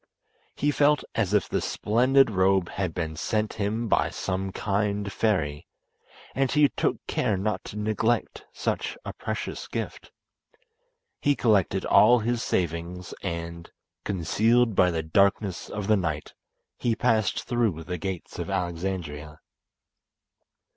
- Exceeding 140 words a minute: No, slow, 135 wpm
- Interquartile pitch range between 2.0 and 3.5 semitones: No, average, 4.2 semitones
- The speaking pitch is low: Yes, low, 100 Hz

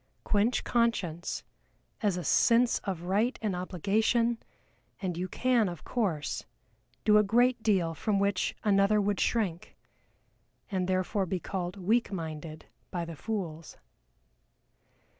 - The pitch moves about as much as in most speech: Yes, average, 3.8 semitones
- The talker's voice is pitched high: Yes, high, 195 Hz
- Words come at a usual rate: No, slow, 125 wpm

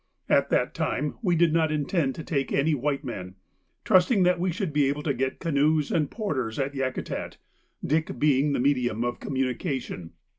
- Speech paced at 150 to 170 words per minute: No, average, 180 wpm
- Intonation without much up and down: No, average, 3.5 semitones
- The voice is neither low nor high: Yes, medium, 145 Hz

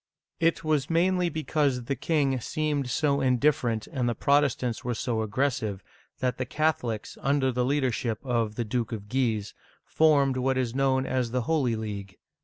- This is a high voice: No, low, 130 Hz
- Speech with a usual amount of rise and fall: Yes, average, 3.6 semitones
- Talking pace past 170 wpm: No, average, 165 wpm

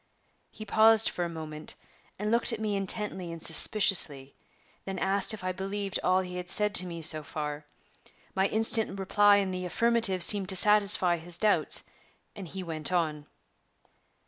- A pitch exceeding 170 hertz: Yes, high, 190 Hz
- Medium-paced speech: Yes, average, 170 wpm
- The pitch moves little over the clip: No, average, 3.5 semitones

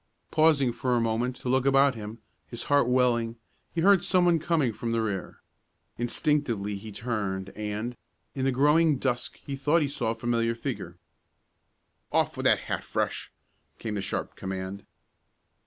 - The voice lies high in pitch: No, low, 120 Hz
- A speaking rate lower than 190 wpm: Yes, average, 160 wpm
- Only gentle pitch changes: No, average, 4.1 semitones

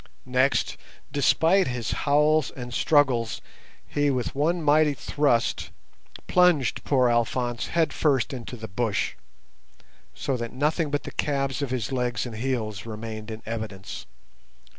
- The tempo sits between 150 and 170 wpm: No, slow, 135 wpm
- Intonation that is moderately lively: Yes, average, 4.0 semitones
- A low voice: Yes, low, 130 Hz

